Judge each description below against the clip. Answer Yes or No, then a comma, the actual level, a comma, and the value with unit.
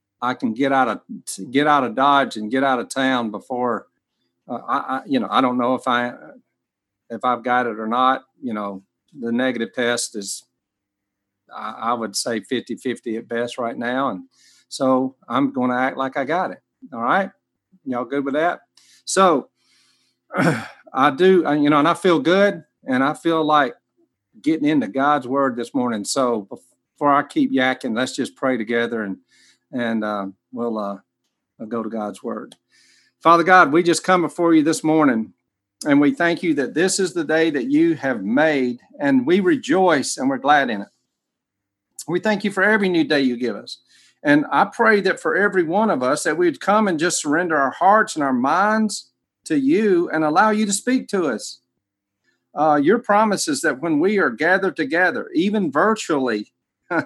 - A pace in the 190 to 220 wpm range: Yes, average, 195 wpm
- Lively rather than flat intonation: Yes, wide, 7.7 semitones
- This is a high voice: No, medium, 140 Hz